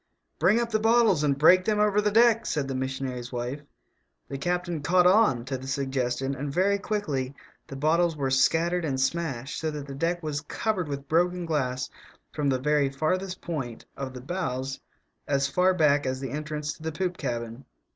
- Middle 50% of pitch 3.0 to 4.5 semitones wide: No, average, 5.0 semitones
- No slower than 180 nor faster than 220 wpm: Yes, average, 195 wpm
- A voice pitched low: No, medium, 150 Hz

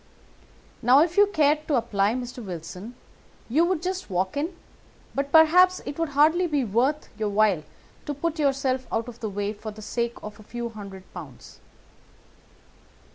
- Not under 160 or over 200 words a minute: Yes, average, 170 wpm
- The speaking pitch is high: Yes, very high, 250 Hz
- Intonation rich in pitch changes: Yes, wide, 6.5 semitones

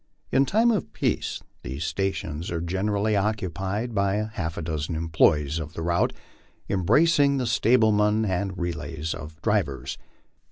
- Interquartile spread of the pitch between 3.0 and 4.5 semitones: No, average, 5.0 semitones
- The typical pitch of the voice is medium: No, very low, 95 Hz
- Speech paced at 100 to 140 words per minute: Yes, slow, 135 wpm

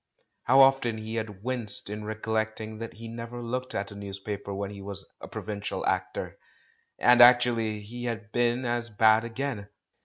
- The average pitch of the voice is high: No, low, 110 Hz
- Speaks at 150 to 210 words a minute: Yes, average, 165 wpm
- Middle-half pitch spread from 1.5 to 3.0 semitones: Yes, narrow, 2.5 semitones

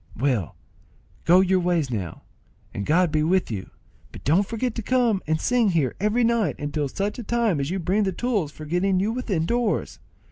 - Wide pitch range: Yes, wide, 6.0 semitones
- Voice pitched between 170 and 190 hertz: Yes, medium, 185 Hz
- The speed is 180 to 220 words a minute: Yes, average, 190 wpm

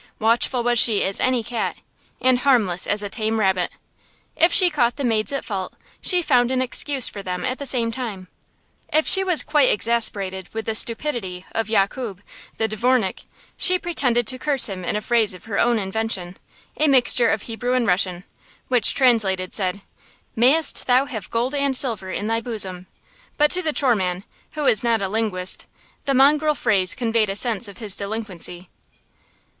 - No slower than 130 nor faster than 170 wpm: No, average, 180 wpm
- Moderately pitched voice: No, high, 230 Hz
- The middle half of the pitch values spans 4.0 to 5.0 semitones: Yes, average, 4.5 semitones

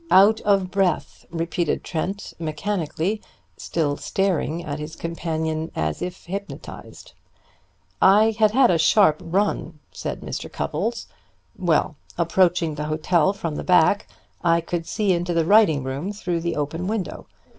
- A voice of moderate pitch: Yes, medium, 170 Hz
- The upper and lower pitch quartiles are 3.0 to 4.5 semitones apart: Yes, average, 3.6 semitones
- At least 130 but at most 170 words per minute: Yes, average, 140 wpm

